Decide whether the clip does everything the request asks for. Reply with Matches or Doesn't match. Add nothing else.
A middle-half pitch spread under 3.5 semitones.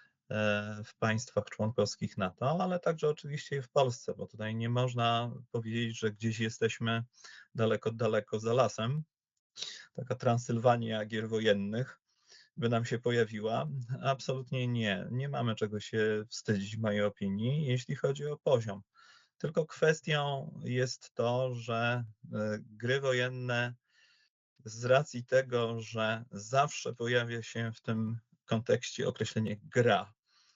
Matches